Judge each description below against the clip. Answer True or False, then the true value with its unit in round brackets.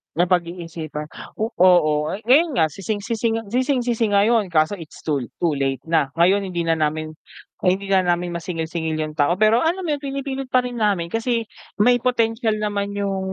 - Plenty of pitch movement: True (5.8 semitones)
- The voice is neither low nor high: False (195 Hz)